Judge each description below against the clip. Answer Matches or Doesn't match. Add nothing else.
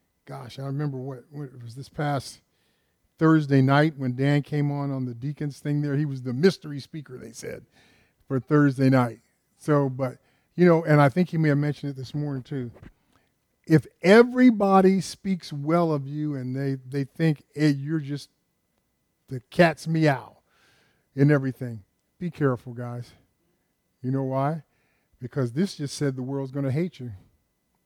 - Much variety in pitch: Doesn't match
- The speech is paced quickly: Doesn't match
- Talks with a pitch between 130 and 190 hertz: Matches